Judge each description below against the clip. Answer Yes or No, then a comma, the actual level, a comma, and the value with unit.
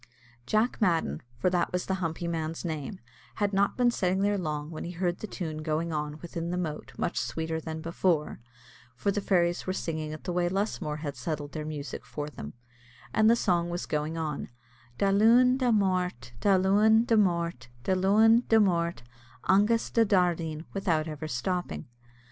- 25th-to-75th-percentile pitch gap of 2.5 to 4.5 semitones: Yes, average, 4.0 semitones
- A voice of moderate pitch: Yes, medium, 175 Hz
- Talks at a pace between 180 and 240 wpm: Yes, average, 185 wpm